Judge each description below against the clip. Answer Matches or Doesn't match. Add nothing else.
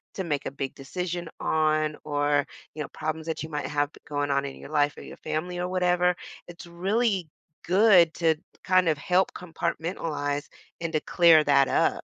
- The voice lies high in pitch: Doesn't match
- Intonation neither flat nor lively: Matches